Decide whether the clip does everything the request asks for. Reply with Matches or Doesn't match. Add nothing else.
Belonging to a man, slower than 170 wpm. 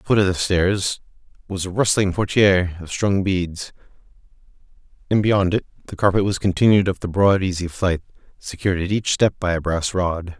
Doesn't match